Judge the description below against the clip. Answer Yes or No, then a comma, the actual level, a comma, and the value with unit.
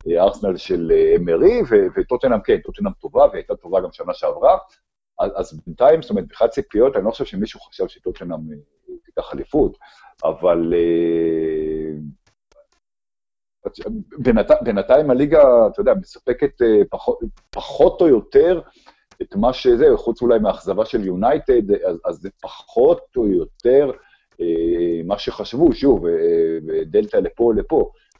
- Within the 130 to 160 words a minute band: No, average, 115 wpm